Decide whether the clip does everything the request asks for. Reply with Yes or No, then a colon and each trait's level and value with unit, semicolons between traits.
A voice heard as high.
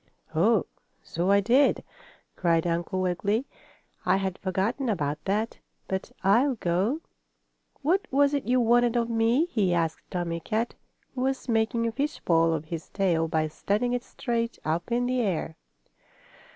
Yes: high, 210 Hz